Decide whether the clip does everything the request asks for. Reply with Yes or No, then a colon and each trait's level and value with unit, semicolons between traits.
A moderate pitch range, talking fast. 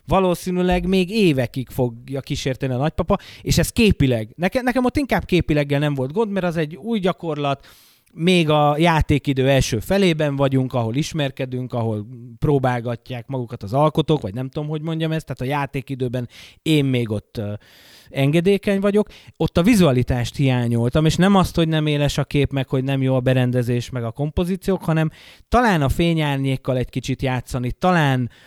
Yes: average, 4.8 semitones; fast, 165 wpm